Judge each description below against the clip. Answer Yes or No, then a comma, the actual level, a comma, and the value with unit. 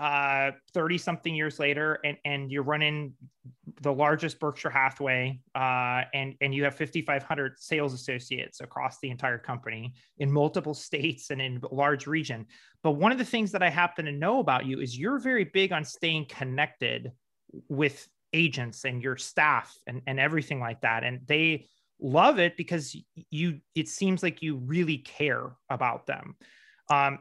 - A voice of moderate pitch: Yes, medium, 145 Hz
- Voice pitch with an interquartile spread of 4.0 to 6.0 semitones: No, average, 3.1 semitones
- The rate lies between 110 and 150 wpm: No, average, 170 wpm